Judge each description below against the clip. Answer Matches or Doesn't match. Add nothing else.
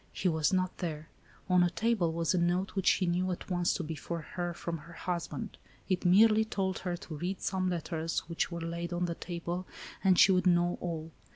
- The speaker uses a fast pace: Matches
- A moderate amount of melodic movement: Doesn't match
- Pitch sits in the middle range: Matches